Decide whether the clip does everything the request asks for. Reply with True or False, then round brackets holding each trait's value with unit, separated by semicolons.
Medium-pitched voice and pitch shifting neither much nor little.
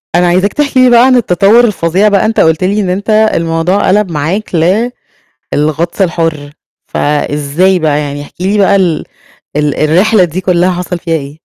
True (180 Hz; 4.2 semitones)